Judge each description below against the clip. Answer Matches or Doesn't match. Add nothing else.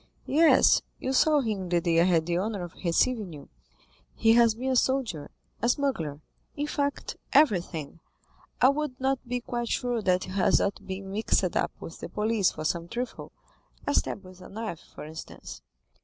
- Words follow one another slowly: Doesn't match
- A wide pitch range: Matches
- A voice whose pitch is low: Doesn't match